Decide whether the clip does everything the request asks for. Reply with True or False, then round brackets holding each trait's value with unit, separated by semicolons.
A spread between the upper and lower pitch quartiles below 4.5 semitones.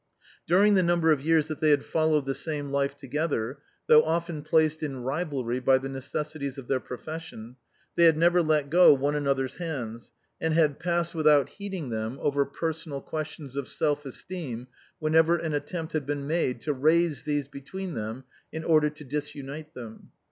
True (3.0 semitones)